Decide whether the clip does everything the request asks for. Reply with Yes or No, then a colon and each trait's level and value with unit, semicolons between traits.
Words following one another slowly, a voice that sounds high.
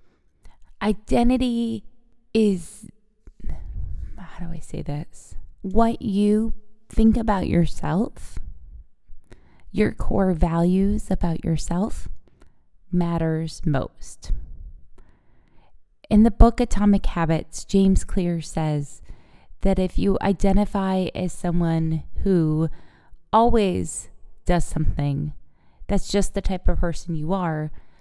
No: slow, 95 wpm; medium, 180 Hz